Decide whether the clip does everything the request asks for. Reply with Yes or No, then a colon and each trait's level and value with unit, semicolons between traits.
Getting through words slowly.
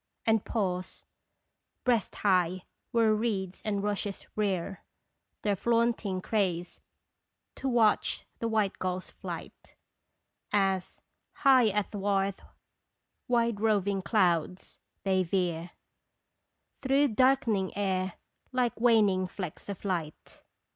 Yes: slow, 100 wpm